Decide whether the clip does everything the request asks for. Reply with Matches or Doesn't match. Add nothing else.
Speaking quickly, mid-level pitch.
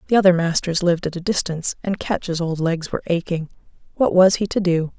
Matches